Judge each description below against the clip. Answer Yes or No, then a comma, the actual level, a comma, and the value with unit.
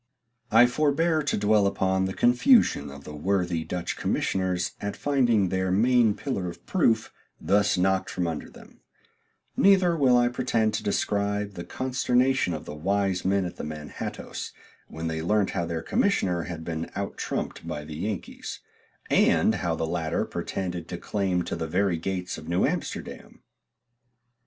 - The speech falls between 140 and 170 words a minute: Yes, average, 160 wpm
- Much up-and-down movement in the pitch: No, average, 4.7 semitones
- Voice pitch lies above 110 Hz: No, very low, 95 Hz